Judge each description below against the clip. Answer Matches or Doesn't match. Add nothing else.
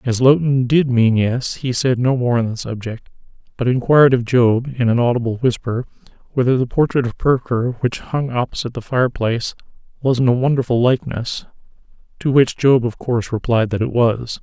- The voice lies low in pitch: Matches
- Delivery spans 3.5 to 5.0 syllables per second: Doesn't match